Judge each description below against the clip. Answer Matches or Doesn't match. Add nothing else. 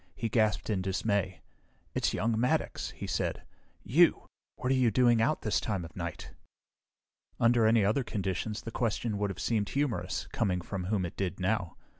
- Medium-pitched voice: Doesn't match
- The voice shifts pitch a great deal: Doesn't match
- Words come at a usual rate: Matches